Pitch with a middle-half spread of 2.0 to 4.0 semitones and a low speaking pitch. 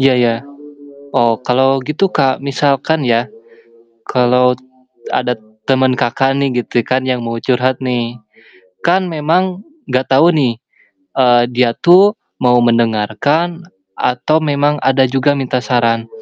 Yes: average, 2.8 semitones; low, 130 Hz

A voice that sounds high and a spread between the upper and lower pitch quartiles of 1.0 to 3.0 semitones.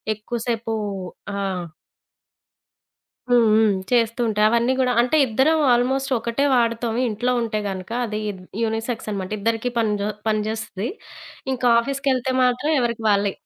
Yes: high, 230 Hz; narrow, 2.4 semitones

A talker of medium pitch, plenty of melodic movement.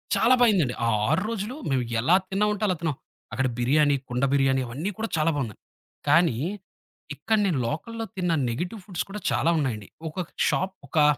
Yes: medium, 160 Hz; wide, 6.7 semitones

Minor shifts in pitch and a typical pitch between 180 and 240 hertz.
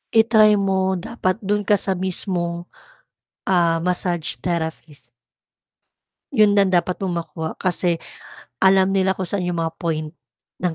Yes: narrow, 2.2 semitones; medium, 185 Hz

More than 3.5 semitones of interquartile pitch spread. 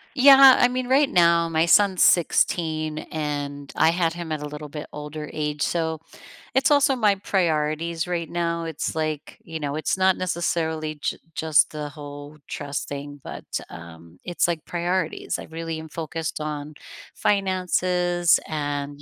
No: average, 2.9 semitones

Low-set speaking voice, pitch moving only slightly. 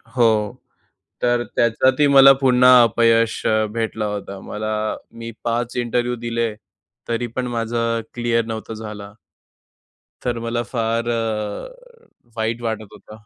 Yes: low, 115 Hz; narrow, 1.6 semitones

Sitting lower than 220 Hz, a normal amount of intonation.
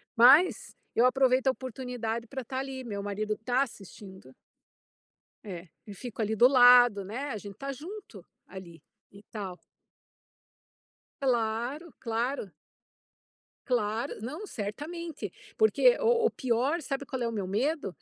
No: high, 245 Hz; average, 4.4 semitones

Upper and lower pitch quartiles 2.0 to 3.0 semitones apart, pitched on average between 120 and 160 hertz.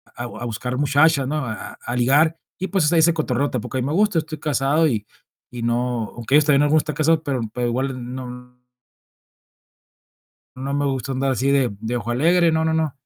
No: average, 3.9 semitones; low, 135 Hz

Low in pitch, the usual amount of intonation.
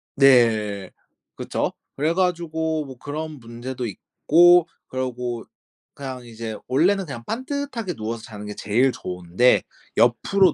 No: low, 130 Hz; wide, 5.8 semitones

